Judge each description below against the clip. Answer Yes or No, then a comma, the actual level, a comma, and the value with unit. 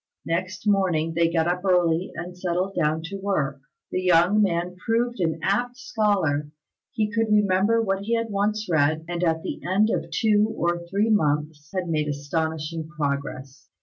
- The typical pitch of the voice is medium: Yes, medium, 180 Hz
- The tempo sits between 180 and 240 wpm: No, average, 170 wpm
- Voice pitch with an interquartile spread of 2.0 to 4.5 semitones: Yes, average, 4.2 semitones